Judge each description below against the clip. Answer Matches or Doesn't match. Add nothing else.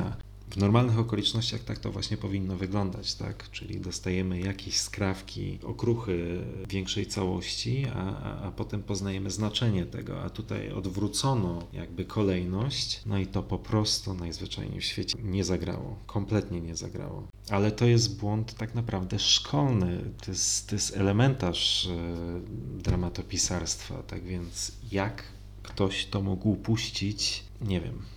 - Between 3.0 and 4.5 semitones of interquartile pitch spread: Doesn't match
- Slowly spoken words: Doesn't match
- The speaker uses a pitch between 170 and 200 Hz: Doesn't match